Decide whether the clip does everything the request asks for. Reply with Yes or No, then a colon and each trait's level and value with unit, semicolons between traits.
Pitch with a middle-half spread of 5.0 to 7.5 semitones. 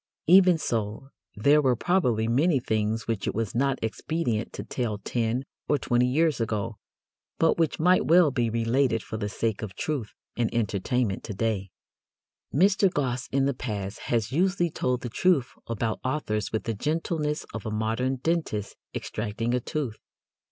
Yes: average, 5.3 semitones